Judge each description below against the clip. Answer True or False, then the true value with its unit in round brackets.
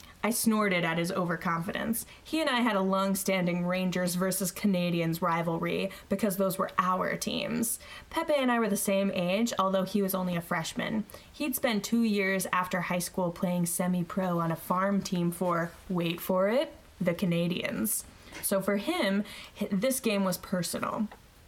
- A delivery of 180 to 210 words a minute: False (170 wpm)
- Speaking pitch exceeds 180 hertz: True (190 Hz)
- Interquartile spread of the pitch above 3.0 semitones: False (2.6 semitones)